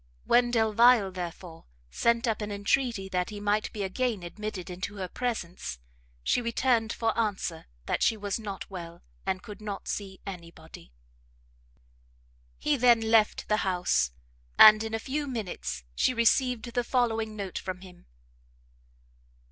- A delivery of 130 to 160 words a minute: Yes, average, 150 wpm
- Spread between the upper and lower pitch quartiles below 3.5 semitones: No, average, 3.8 semitones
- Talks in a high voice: Yes, high, 210 Hz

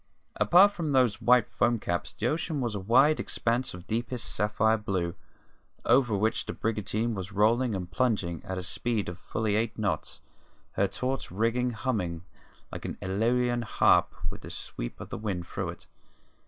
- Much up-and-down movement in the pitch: No, average, 3.9 semitones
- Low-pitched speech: Yes, low, 110 Hz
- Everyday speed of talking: Yes, average, 170 wpm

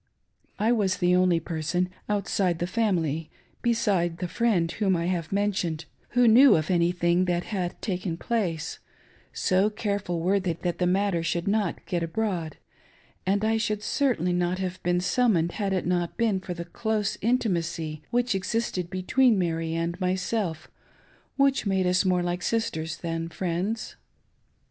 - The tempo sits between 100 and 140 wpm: No, average, 160 wpm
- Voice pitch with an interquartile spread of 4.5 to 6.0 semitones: No, average, 3.4 semitones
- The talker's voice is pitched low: No, medium, 185 Hz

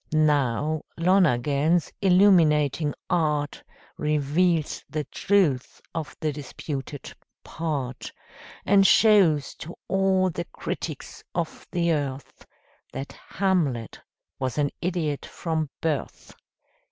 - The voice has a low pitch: No, medium, 155 Hz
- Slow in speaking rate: Yes, slow, 95 wpm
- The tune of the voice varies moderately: Yes, average, 3.6 semitones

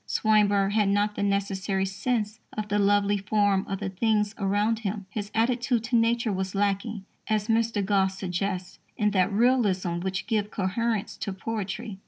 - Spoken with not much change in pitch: Yes, narrow, 2.1 semitones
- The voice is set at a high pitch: Yes, high, 205 Hz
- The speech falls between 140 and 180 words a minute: Yes, average, 165 wpm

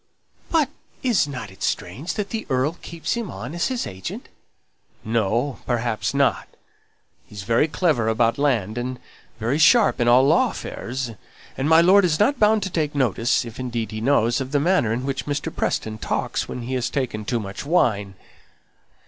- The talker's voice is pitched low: Yes, low, 130 Hz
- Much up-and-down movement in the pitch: Yes, wide, 6.0 semitones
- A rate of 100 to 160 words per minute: No, average, 175 wpm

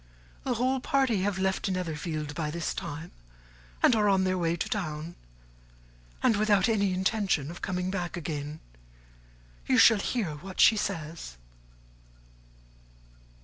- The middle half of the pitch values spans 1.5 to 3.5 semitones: No, average, 4.3 semitones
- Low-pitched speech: No, medium, 185 Hz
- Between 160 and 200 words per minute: No, slow, 135 wpm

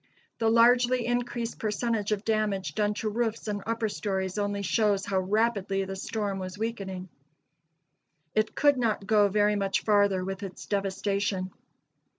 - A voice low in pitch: No, high, 210 Hz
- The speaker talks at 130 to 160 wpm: Yes, average, 150 wpm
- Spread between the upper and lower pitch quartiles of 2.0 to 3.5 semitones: Yes, narrow, 2.4 semitones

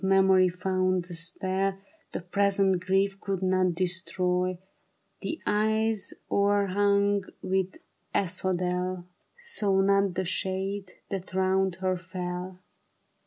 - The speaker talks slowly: Yes, slow, 105 wpm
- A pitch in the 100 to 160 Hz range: No, high, 190 Hz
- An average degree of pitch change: No, narrow, 1.3 semitones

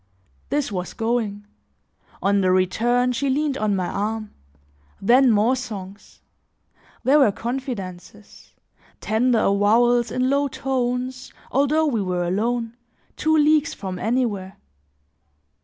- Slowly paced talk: Yes, slow, 115 wpm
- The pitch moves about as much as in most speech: Yes, average, 4.3 semitones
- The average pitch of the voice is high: Yes, high, 235 Hz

